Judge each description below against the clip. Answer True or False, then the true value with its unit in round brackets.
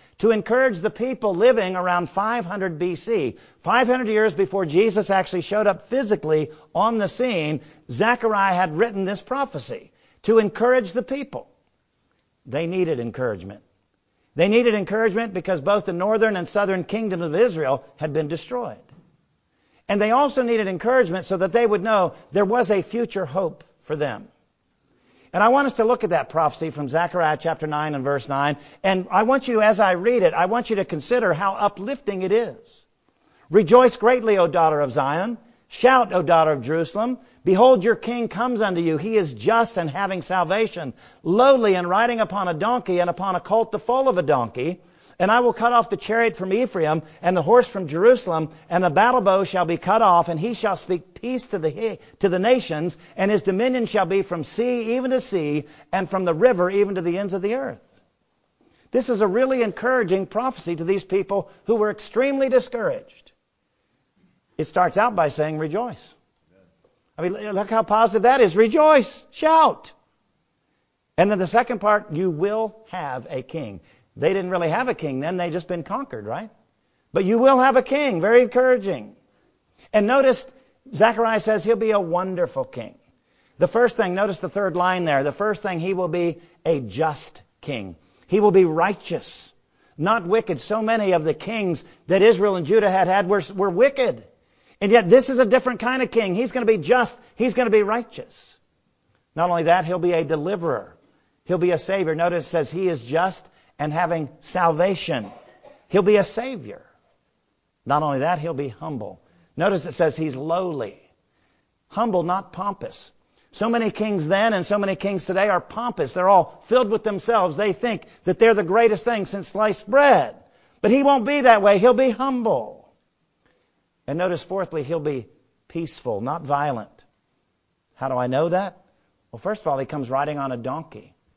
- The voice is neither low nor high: False (195 Hz)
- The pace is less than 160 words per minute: False (185 wpm)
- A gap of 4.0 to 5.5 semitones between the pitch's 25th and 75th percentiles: True (5.1 semitones)